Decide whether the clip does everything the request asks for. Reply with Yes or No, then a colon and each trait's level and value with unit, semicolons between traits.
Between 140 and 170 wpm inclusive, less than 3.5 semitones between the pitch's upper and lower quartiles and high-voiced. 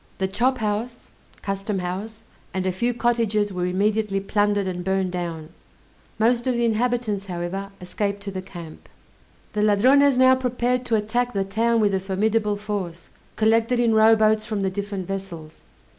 Yes: average, 160 wpm; average, 3.1 semitones; high, 210 Hz